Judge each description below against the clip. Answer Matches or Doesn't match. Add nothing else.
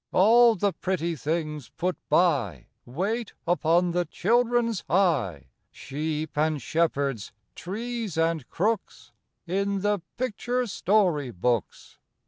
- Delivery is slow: Matches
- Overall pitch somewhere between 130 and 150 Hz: Doesn't match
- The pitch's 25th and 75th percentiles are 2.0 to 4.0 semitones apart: Doesn't match